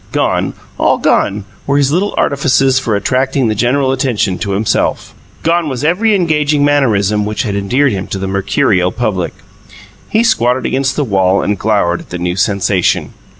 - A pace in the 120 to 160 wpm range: No, average, 170 wpm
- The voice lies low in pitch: Yes, low, 120 Hz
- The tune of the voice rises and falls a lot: Yes, wide, 6.1 semitones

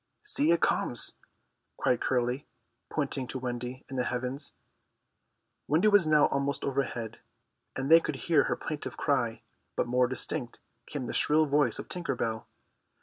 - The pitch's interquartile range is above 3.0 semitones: Yes, average, 3.5 semitones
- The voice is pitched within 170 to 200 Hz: No, low, 135 Hz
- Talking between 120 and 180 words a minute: Yes, average, 150 wpm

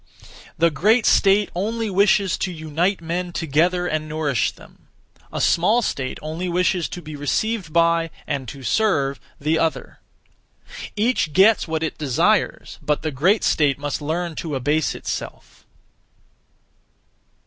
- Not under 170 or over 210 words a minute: No, slow, 135 wpm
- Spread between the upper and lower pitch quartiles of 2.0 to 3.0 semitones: No, average, 4.0 semitones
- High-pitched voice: No, medium, 165 Hz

